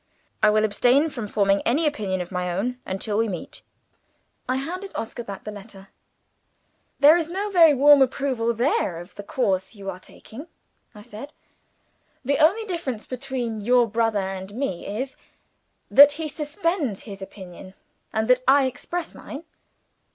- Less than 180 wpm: Yes, average, 160 wpm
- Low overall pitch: No, high, 235 Hz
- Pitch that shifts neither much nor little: No, wide, 6.0 semitones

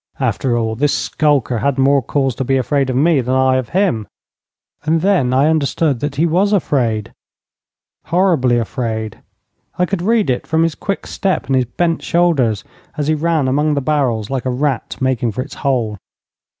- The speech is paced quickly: No, average, 190 wpm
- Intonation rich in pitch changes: No, average, 4.3 semitones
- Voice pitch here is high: No, low, 135 Hz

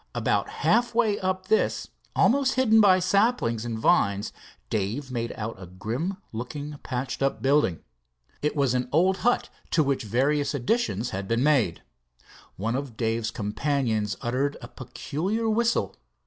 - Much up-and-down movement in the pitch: Yes, wide, 8.5 semitones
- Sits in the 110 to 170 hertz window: Yes, low, 135 Hz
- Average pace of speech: Yes, average, 150 wpm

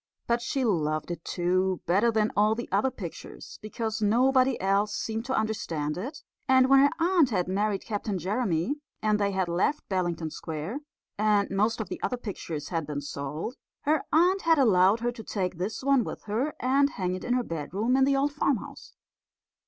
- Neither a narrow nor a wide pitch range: No, wide, 5.9 semitones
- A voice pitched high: Yes, high, 215 Hz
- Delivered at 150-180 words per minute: No, average, 190 wpm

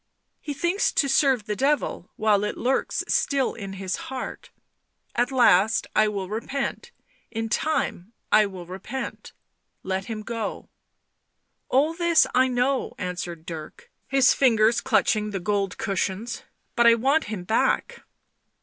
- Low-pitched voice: No, high, 225 Hz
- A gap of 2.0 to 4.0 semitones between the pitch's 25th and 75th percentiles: No, average, 5.1 semitones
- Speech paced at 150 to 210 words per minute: Yes, average, 160 wpm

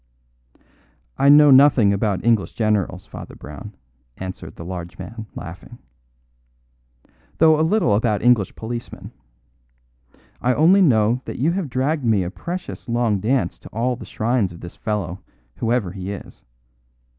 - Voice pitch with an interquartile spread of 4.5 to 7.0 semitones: Yes, average, 4.9 semitones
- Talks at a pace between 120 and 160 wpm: Yes, average, 145 wpm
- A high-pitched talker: No, low, 115 Hz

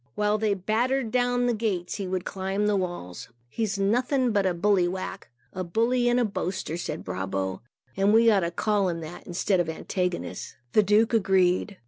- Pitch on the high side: Yes, high, 195 Hz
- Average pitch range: Yes, average, 3.8 semitones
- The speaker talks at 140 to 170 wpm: No, average, 185 wpm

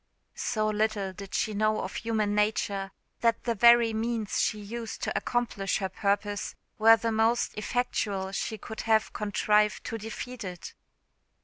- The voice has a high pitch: Yes, high, 215 Hz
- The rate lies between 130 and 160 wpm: Yes, average, 150 wpm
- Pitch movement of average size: No, narrow, 1.8 semitones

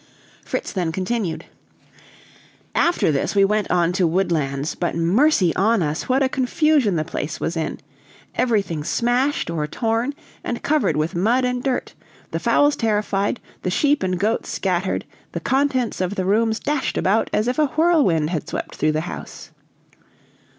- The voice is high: Yes, high, 205 Hz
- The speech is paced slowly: No, average, 160 wpm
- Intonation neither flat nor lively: No, wide, 6.8 semitones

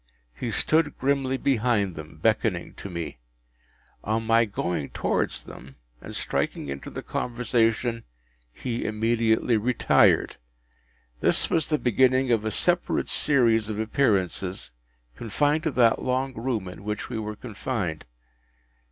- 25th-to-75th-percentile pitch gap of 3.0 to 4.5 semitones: Yes, average, 3.9 semitones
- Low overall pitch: Yes, low, 115 Hz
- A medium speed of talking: No, slow, 130 wpm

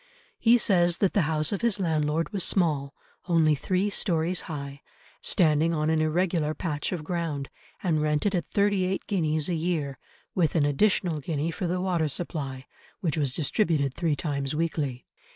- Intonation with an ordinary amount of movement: Yes, average, 3.3 semitones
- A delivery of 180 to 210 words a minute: No, average, 170 wpm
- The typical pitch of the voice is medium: Yes, medium, 160 Hz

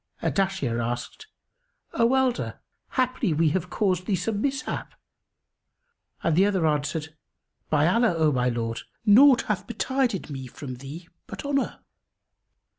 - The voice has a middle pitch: Yes, medium, 180 Hz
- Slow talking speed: Yes, slow, 130 wpm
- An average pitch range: No, wide, 7.9 semitones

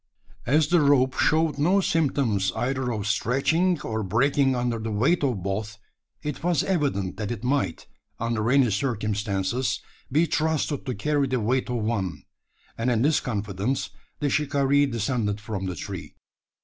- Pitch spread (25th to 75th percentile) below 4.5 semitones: No, average, 5.2 semitones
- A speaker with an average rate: Yes, average, 155 wpm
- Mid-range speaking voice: No, low, 125 Hz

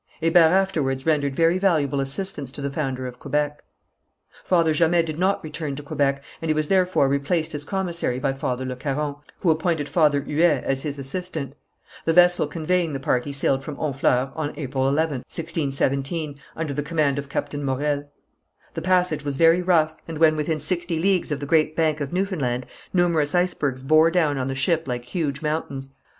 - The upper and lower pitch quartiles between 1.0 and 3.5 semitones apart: Yes, average, 3.1 semitones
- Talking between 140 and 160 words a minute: No, average, 185 wpm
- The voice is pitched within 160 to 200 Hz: No, medium, 150 Hz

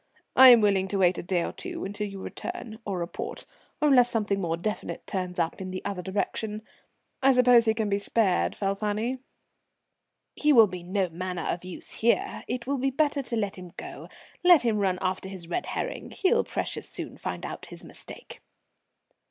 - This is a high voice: Yes, high, 205 Hz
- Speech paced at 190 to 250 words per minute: Yes, average, 195 wpm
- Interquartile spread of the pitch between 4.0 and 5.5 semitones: Yes, average, 4.7 semitones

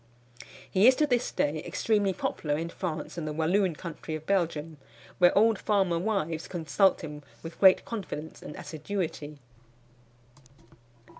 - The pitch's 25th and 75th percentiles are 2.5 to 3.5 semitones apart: No, average, 4.1 semitones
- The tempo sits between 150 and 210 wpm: No, average, 140 wpm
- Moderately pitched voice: Yes, medium, 170 Hz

